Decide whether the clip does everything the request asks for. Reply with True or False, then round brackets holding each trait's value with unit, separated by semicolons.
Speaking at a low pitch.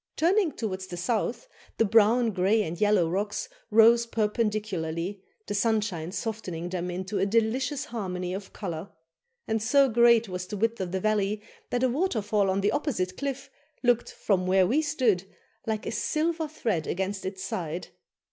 False (210 Hz)